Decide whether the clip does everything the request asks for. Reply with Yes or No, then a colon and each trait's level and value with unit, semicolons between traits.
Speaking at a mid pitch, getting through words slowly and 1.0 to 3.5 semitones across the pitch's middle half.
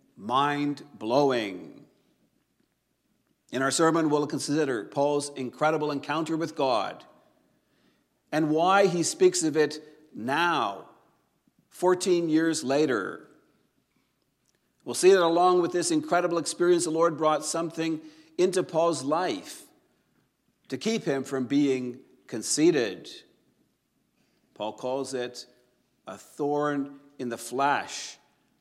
Yes: medium, 155 Hz; slow, 105 wpm; average, 3.1 semitones